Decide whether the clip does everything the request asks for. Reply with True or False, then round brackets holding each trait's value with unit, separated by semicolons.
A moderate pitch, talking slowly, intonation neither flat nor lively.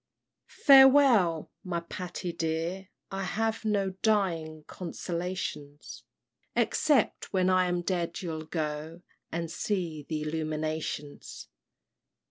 True (175 Hz; 100 wpm; 3.4 semitones)